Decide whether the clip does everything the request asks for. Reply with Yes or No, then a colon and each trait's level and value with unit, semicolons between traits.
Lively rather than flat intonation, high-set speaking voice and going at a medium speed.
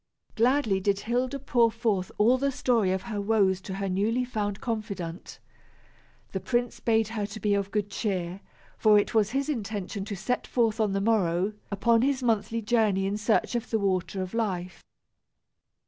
No: average, 3.0 semitones; high, 215 Hz; average, 180 wpm